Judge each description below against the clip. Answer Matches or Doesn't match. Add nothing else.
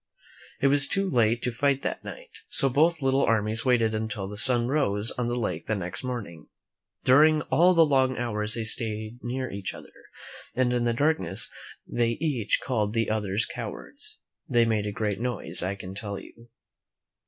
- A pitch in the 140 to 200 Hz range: Doesn't match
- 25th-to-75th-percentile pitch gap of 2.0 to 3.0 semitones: Doesn't match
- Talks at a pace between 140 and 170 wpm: Doesn't match